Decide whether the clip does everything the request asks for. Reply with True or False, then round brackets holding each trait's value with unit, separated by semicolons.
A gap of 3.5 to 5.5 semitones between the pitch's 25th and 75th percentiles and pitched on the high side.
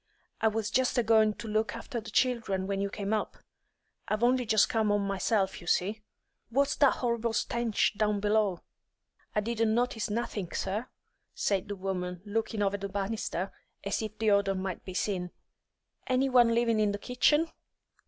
False (2.7 semitones; 215 Hz)